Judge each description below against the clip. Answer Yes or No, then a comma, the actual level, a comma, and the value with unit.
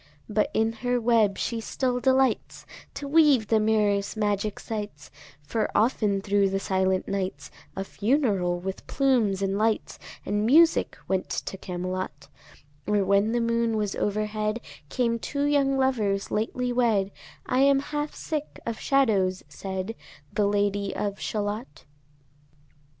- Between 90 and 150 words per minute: Yes, average, 140 wpm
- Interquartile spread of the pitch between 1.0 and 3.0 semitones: No, average, 3.8 semitones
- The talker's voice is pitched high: Yes, high, 215 Hz